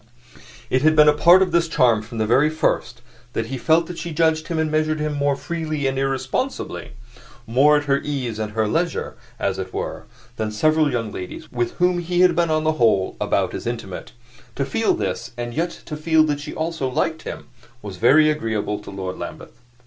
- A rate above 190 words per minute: Yes, fast, 205 wpm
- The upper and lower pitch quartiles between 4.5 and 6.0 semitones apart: Yes, average, 5.0 semitones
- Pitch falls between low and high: Yes, medium, 150 Hz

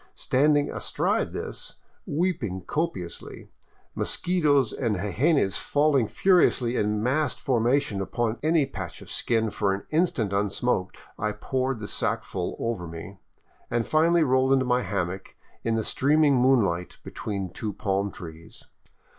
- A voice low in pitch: Yes, low, 120 Hz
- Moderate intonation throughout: No, wide, 6.2 semitones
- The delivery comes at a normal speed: No, slow, 130 wpm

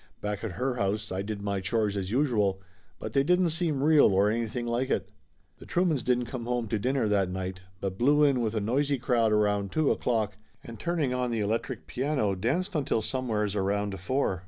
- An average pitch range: Yes, average, 4.7 semitones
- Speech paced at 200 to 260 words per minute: Yes, fast, 205 wpm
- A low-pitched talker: Yes, low, 115 Hz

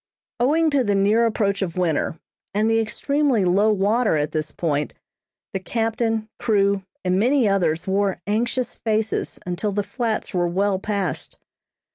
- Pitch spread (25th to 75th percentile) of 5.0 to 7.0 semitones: No, average, 3.2 semitones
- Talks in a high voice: Yes, high, 205 Hz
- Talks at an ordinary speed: Yes, average, 150 wpm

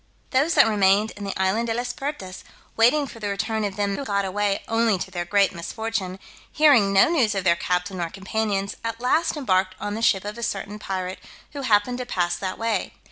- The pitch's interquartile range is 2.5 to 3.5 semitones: Yes, average, 3.2 semitones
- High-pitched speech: Yes, high, 205 Hz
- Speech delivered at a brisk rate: Yes, fast, 215 wpm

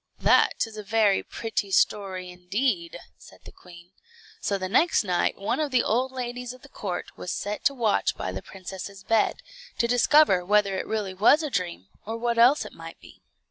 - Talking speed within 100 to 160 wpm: No, average, 195 wpm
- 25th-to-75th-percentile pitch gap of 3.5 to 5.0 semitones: Yes, average, 4.7 semitones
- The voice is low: No, high, 210 Hz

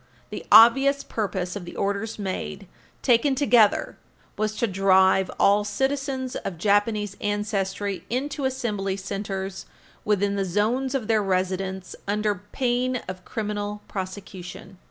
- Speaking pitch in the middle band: No, high, 205 Hz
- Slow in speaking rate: Yes, slow, 125 wpm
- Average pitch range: Yes, average, 3.3 semitones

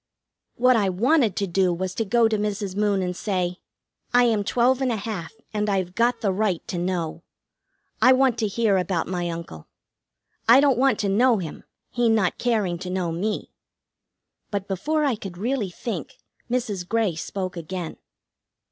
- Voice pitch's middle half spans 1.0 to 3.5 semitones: No, average, 4.4 semitones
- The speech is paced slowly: No, average, 175 wpm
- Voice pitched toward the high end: Yes, high, 200 Hz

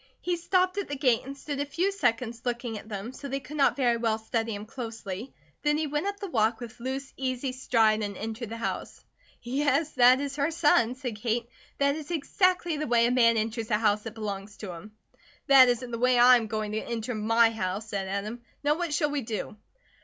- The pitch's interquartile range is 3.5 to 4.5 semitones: Yes, average, 4.2 semitones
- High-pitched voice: Yes, high, 240 Hz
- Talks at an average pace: No, fast, 225 wpm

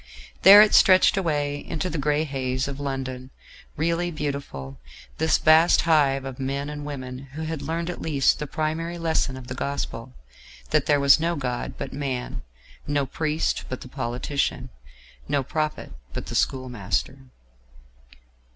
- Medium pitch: Yes, medium, 145 Hz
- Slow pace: No, average, 150 wpm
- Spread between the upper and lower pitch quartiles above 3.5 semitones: No, average, 3.2 semitones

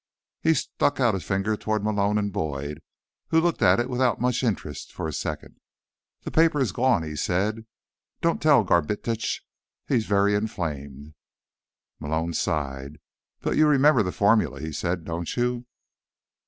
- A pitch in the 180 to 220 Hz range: No, low, 105 Hz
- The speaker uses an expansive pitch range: Yes, wide, 7.2 semitones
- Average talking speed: Yes, average, 155 wpm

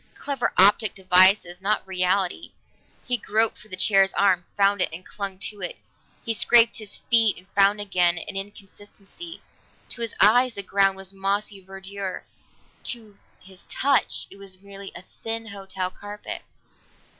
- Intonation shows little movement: Yes, narrow, 1.9 semitones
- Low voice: No, high, 200 Hz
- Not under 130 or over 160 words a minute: Yes, average, 155 wpm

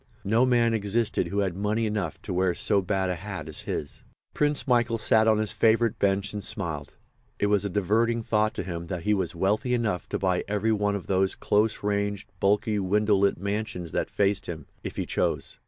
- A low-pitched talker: Yes, low, 100 Hz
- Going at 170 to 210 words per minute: Yes, fast, 205 wpm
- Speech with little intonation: Yes, narrow, 2.3 semitones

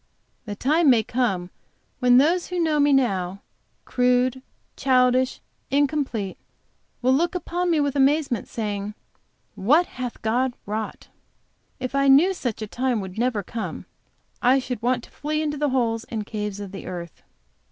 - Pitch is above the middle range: Yes, very high, 250 Hz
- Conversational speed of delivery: Yes, average, 155 wpm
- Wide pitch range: No, average, 4.7 semitones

